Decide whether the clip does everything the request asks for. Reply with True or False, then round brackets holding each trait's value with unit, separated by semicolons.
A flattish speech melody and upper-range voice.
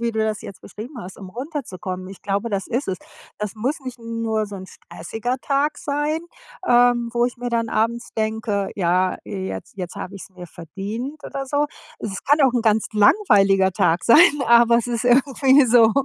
False (4.2 semitones; 230 Hz)